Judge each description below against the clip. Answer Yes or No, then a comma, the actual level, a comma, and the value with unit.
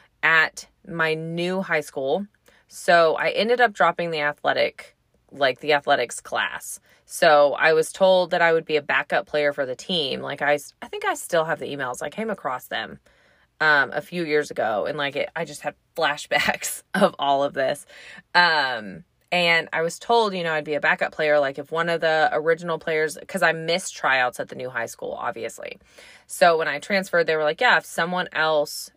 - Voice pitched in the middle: Yes, medium, 160 Hz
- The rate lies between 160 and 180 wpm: No, fast, 205 wpm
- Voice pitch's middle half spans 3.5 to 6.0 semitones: No, average, 2.7 semitones